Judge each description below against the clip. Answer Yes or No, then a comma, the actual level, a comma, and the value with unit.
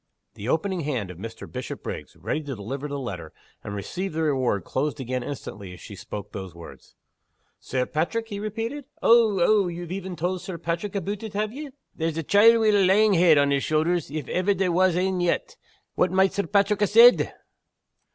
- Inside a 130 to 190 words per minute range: No, average, 200 wpm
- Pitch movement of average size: No, wide, 6.9 semitones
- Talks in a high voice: No, medium, 175 Hz